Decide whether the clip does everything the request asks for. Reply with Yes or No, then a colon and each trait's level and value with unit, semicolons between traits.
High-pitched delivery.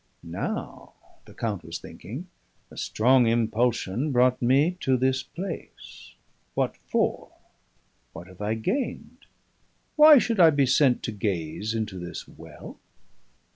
No: low, 125 Hz